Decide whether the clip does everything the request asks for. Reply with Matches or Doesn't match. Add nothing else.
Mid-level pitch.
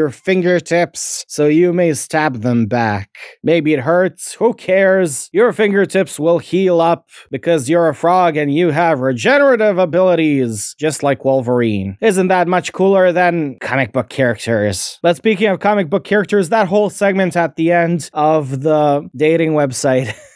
Matches